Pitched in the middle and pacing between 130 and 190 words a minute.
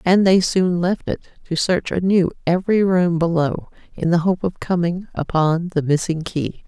Yes: medium, 175 Hz; average, 180 wpm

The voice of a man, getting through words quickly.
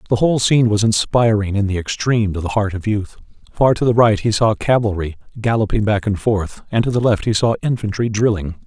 Yes: male; fast, 220 wpm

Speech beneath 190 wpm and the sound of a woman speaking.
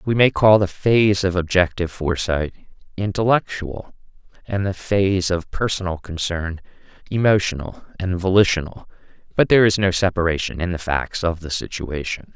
No: average, 140 wpm; male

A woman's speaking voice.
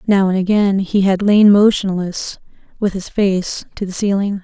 Yes: female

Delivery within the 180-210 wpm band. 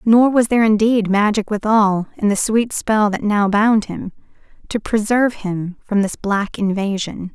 No: average, 170 wpm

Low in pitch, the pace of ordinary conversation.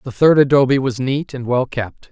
No: low, 130 Hz; fast, 225 wpm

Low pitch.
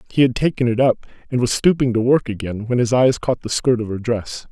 Yes: low, 120 Hz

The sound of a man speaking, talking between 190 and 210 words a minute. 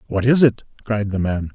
No: male; fast, 235 wpm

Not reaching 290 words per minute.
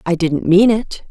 Yes: fast, 220 wpm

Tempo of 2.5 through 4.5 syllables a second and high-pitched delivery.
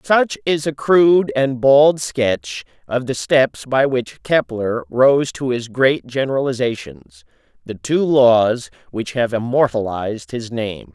No: 3.7 syllables/s; low, 130 Hz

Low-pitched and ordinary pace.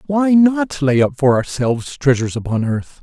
No: medium, 145 Hz; average, 180 wpm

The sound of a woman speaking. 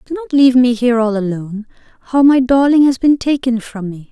Yes: female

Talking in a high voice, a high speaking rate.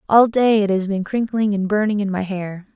Yes: high, 205 Hz; fast, 240 wpm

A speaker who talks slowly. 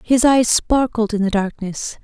No: average, 175 wpm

